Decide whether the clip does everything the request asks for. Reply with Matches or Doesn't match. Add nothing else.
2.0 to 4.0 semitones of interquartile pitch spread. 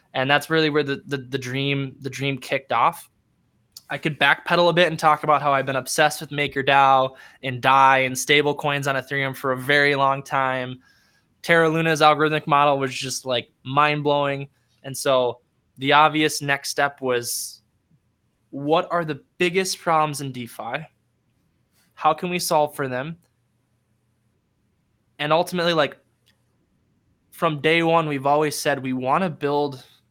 Matches